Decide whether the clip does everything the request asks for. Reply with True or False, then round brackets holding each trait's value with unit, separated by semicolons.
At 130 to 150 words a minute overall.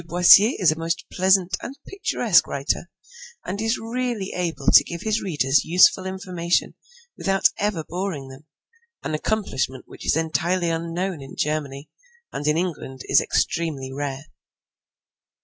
True (140 wpm)